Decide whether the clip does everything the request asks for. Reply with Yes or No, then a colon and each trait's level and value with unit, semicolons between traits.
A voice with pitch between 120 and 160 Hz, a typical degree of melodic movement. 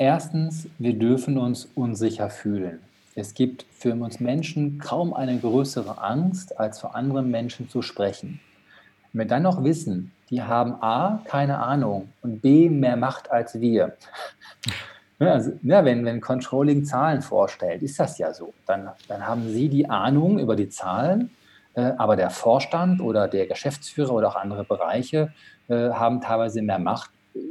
Yes: low, 125 Hz; average, 4.2 semitones